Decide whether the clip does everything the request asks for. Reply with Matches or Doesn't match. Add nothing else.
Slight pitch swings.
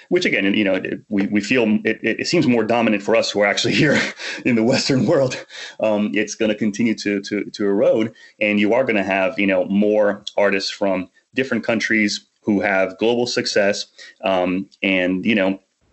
Matches